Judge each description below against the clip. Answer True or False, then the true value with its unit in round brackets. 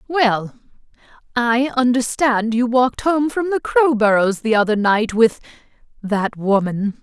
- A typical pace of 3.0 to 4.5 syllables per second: True (4.1 syllables/s)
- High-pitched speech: True (235 Hz)